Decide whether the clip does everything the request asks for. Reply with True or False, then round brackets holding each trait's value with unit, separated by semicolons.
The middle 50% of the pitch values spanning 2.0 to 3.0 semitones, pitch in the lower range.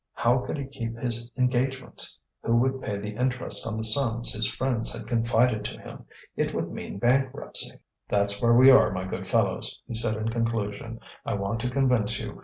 True (2.6 semitones; 115 Hz)